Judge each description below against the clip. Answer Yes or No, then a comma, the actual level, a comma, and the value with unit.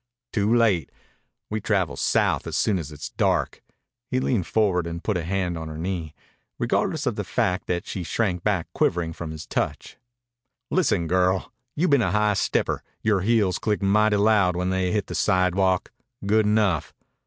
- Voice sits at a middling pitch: No, very low, 95 Hz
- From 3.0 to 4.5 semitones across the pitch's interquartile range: Yes, average, 3.4 semitones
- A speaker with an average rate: Yes, average, 175 wpm